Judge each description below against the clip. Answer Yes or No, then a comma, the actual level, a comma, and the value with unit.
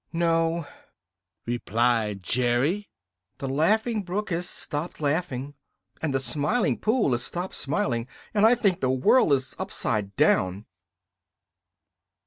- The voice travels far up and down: Yes, wide, 6.7 semitones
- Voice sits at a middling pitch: Yes, medium, 145 Hz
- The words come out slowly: Yes, slow, 115 wpm